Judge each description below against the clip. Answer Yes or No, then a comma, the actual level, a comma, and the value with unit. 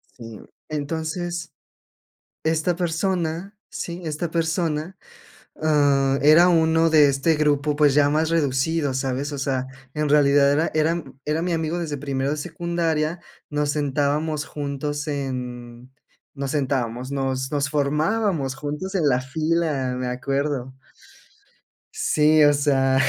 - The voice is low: No, medium, 150 Hz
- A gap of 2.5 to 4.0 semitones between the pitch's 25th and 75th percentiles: Yes, average, 2.8 semitones